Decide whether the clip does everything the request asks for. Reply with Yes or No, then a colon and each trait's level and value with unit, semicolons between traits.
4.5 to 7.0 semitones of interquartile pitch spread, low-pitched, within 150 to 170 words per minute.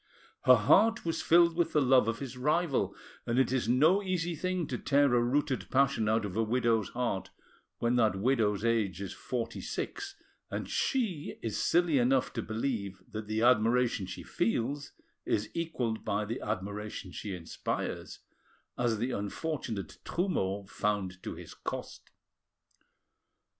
Yes: average, 5.3 semitones; low, 120 Hz; average, 155 wpm